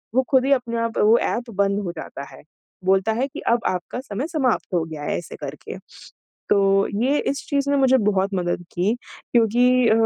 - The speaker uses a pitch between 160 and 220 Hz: No, high, 230 Hz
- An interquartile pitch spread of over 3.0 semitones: Yes, average, 5.3 semitones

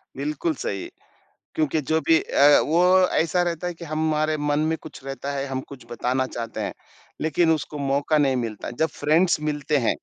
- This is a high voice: No, medium, 150 Hz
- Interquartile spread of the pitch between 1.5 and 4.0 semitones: Yes, average, 2.7 semitones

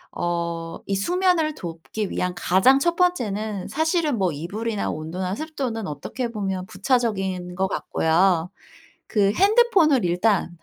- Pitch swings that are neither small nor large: No, wide, 7.4 semitones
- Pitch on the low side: No, high, 200 Hz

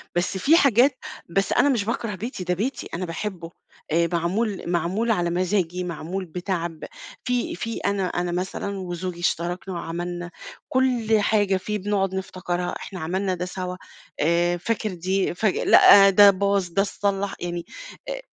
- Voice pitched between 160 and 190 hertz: Yes, medium, 185 Hz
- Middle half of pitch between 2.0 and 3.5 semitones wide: Yes, average, 2.8 semitones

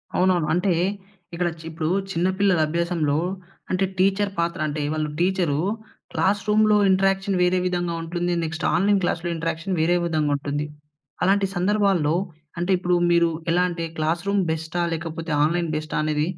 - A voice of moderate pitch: Yes, medium, 175 Hz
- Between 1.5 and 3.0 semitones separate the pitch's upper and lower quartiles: Yes, average, 2.7 semitones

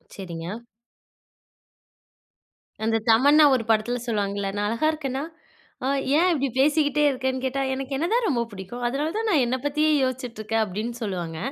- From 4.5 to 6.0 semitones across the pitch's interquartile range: Yes, average, 5.1 semitones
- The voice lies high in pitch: Yes, very high, 255 Hz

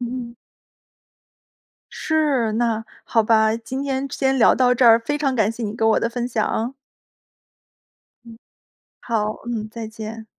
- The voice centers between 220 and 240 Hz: Yes, high, 235 Hz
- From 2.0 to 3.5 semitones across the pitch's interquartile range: Yes, narrow, 2.4 semitones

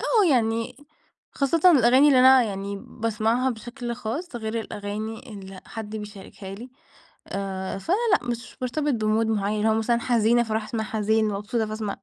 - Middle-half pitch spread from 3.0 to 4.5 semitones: No, narrow, 2.6 semitones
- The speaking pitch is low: No, high, 225 Hz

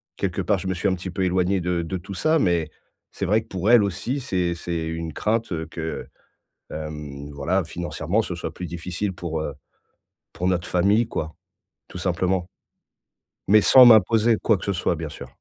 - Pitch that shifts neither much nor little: Yes, average, 3.0 semitones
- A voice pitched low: Yes, very low, 90 Hz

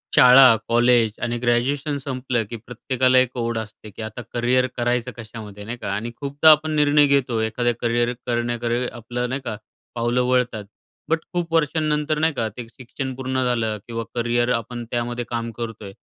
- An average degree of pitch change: No, narrow, 2.0 semitones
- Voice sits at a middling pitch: No, low, 120 Hz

